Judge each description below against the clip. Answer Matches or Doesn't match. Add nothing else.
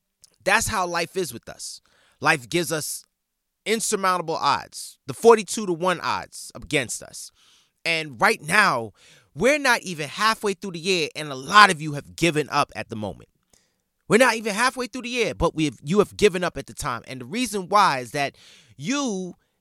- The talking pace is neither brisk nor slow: Matches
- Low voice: Doesn't match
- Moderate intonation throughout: Doesn't match